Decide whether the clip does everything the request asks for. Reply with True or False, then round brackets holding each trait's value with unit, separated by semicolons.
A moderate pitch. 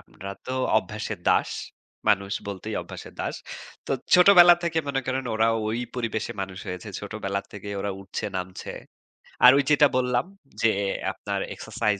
False (110 Hz)